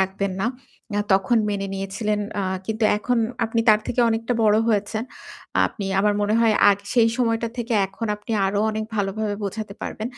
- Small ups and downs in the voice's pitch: Yes, narrow, 2.1 semitones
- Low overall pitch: No, high, 215 Hz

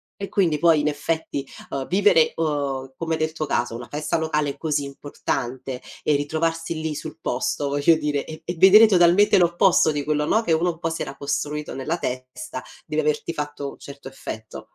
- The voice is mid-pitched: Yes, medium, 150 Hz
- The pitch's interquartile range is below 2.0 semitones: No, average, 2.7 semitones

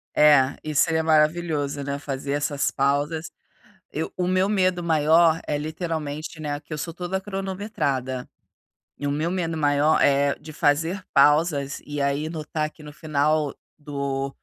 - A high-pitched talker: No, medium, 150 Hz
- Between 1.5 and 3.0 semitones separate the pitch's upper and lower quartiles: Yes, narrow, 2.5 semitones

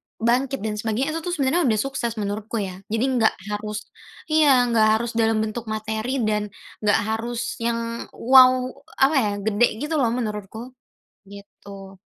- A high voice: Yes, high, 225 Hz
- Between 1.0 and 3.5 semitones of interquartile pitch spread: Yes, average, 3.1 semitones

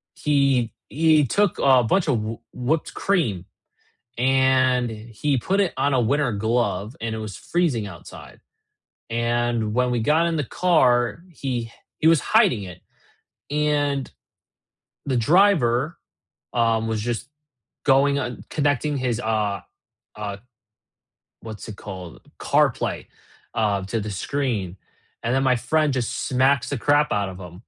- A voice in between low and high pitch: No, low, 125 Hz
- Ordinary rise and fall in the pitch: Yes, average, 4.5 semitones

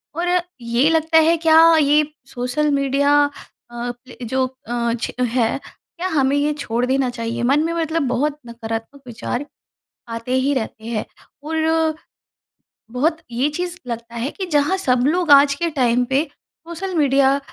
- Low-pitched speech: No, very high, 275 Hz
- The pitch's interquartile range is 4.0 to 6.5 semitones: Yes, average, 4.7 semitones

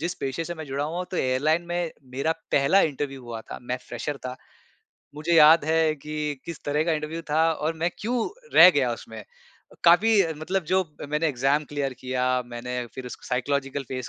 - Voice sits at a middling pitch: Yes, medium, 150 Hz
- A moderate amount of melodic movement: Yes, average, 3.8 semitones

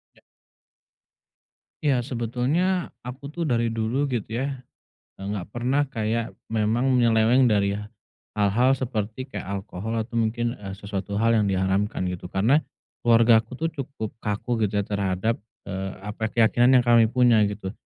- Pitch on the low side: Yes, low, 115 Hz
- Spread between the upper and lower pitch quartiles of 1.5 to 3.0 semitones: No, average, 3.4 semitones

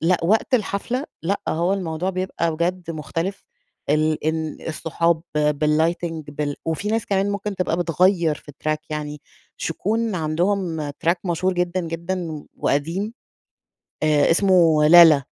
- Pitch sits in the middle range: Yes, medium, 170 Hz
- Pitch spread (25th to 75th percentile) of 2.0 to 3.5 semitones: Yes, average, 3.2 semitones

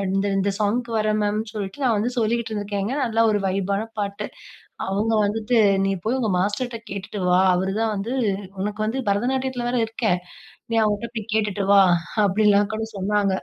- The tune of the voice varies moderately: No, narrow, 2.2 semitones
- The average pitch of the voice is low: No, high, 210 Hz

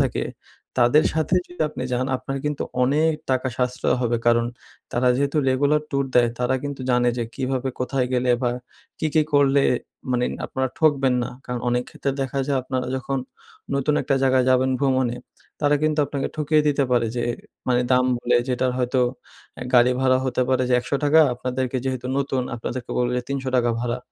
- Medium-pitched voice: No, low, 130 Hz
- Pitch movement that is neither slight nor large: No, narrow, 2.0 semitones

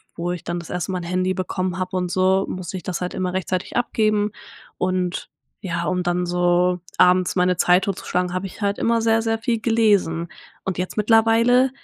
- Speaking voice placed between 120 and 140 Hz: No, medium, 185 Hz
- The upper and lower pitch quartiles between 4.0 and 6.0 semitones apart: No, average, 2.8 semitones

